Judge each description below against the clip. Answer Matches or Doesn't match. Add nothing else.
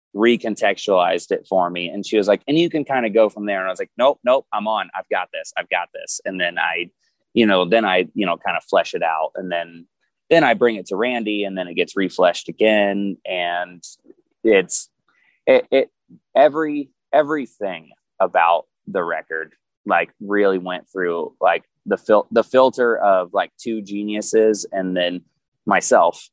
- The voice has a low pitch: Matches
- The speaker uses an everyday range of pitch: Doesn't match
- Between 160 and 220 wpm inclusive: Matches